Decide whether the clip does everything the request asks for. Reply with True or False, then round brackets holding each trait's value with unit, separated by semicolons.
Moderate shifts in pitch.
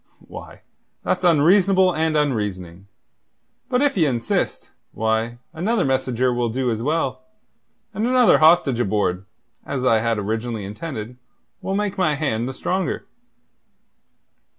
False (7.9 semitones)